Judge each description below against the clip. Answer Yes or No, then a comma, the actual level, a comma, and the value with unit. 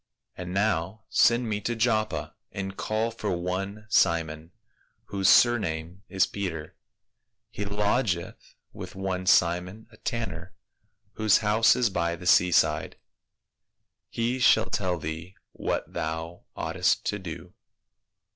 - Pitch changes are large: No, average, 4.0 semitones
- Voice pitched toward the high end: No, very low, 95 Hz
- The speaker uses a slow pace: Yes, slow, 125 wpm